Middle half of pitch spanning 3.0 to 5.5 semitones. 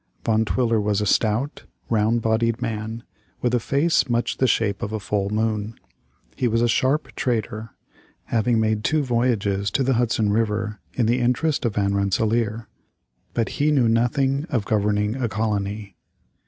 No: narrow, 2.5 semitones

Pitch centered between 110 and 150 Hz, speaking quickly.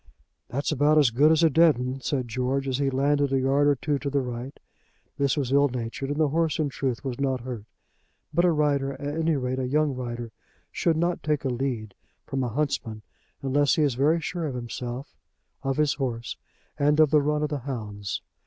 Yes: medium, 140 Hz; fast, 210 wpm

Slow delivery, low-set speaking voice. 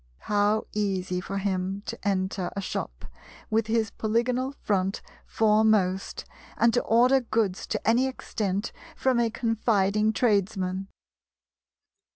No: slow, 120 wpm; high, 210 Hz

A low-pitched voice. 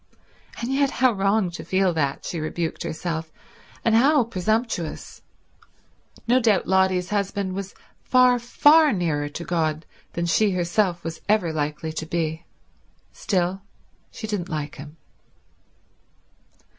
No: medium, 185 Hz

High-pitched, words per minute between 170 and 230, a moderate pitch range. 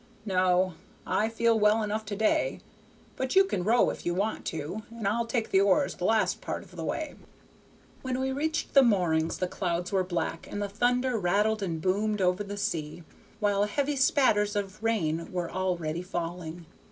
Yes: high, 205 Hz; average, 185 wpm; average, 4.0 semitones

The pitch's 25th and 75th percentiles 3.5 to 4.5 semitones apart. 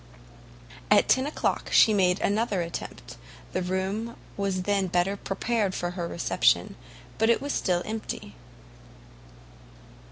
No: average, 3.1 semitones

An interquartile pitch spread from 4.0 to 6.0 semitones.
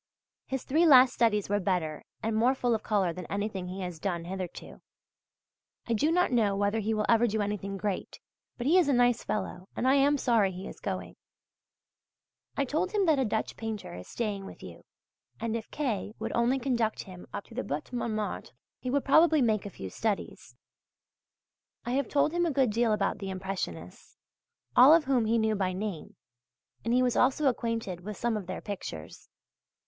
Yes: average, 4.5 semitones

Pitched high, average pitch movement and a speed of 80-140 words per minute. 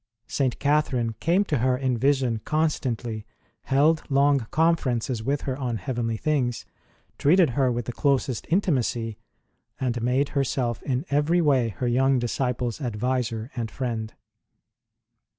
No: low, 130 Hz; average, 3.2 semitones; slow, 135 wpm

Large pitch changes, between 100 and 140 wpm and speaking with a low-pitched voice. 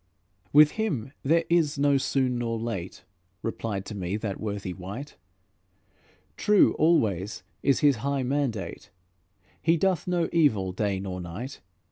Yes: wide, 6.7 semitones; slow, 135 wpm; low, 120 Hz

